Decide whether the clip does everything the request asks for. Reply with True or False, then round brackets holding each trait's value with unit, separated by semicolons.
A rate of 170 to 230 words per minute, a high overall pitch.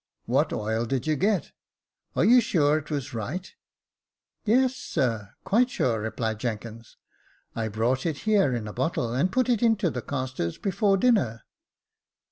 False (175 wpm; 140 Hz)